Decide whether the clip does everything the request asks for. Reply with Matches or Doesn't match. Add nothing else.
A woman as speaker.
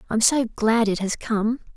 Matches